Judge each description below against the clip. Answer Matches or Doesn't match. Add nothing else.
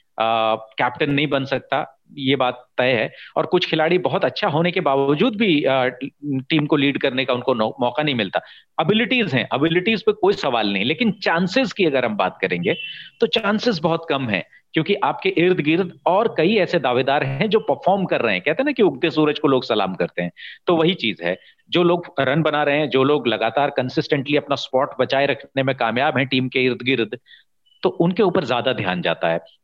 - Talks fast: Matches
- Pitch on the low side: Doesn't match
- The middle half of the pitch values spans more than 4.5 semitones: Matches